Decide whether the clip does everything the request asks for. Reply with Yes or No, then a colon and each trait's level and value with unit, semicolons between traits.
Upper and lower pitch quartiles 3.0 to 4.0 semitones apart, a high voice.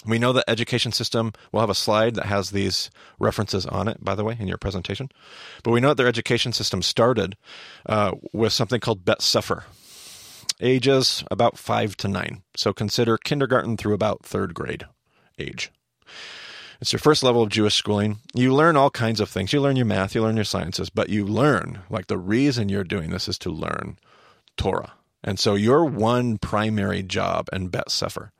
No: average, 3.3 semitones; low, 110 Hz